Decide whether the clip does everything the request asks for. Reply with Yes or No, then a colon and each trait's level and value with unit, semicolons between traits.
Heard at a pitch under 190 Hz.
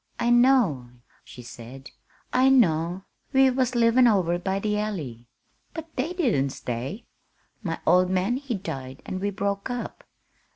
No: high, 200 Hz